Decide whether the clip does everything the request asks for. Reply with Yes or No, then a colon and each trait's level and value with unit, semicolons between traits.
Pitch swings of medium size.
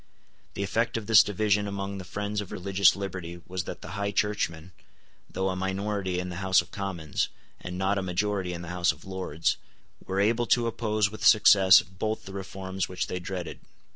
No: narrow, 2.0 semitones